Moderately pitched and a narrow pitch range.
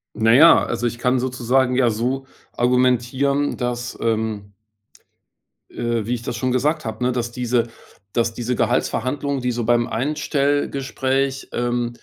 No: low, 125 Hz; narrow, 2.0 semitones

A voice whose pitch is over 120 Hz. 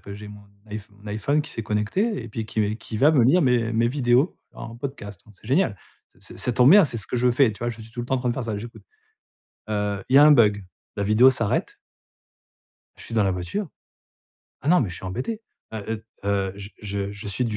No: low, 115 Hz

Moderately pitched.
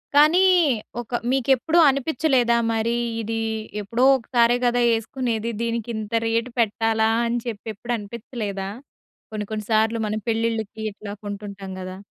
No: high, 225 Hz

